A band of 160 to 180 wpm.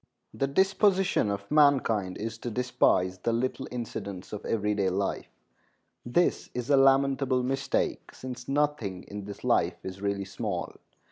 No: average, 145 wpm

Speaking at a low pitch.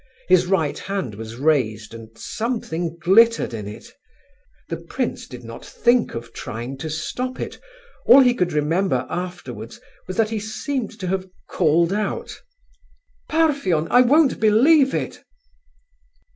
No: medium, 180 Hz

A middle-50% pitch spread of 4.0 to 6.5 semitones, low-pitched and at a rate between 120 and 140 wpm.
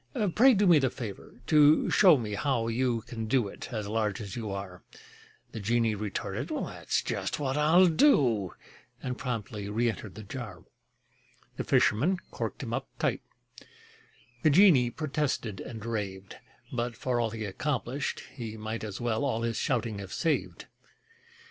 No: average, 4.4 semitones; low, 115 Hz; average, 155 wpm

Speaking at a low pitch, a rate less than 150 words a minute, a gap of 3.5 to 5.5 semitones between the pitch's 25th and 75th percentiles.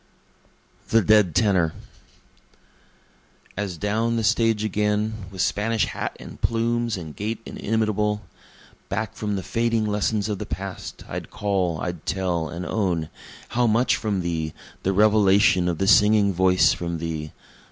No: low, 105 Hz; average, 140 wpm; average, 3.1 semitones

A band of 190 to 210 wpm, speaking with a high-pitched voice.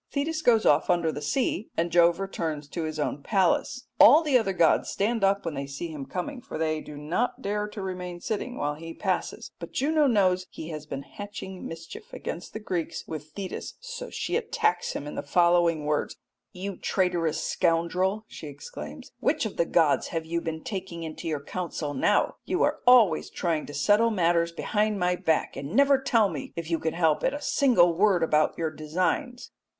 No: average, 195 wpm; medium, 175 Hz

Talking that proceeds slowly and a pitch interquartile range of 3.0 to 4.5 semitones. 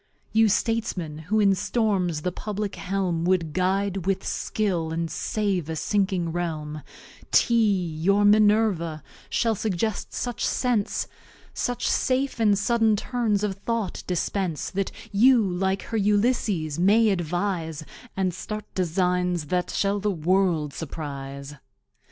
Yes: slow, 125 wpm; average, 3.9 semitones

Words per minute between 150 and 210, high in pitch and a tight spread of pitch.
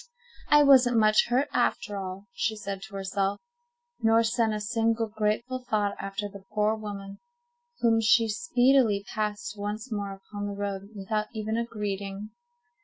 Yes: average, 155 wpm; high, 215 Hz; narrow, 2.1 semitones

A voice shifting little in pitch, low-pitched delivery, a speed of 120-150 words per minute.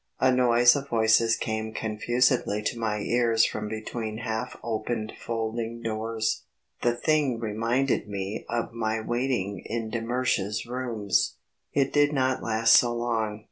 Yes: narrow, 1.8 semitones; low, 115 Hz; average, 140 wpm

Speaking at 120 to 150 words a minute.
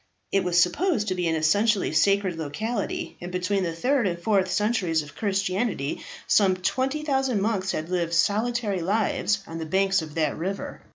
No: average, 170 wpm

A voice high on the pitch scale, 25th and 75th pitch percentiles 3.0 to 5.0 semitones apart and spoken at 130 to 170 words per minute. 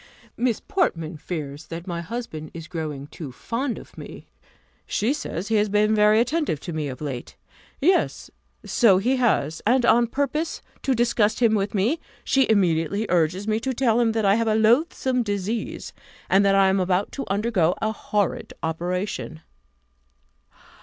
No: high, 210 Hz; wide, 5.6 semitones; average, 165 wpm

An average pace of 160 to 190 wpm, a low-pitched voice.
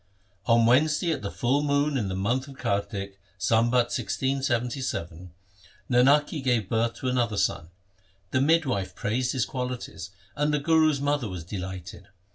No: average, 145 wpm; low, 125 Hz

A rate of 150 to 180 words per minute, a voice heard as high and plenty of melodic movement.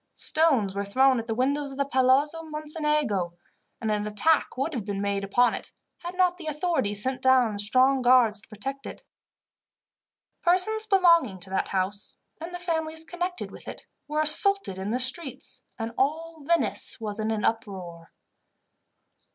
Yes: average, 165 wpm; very high, 260 Hz; wide, 7.3 semitones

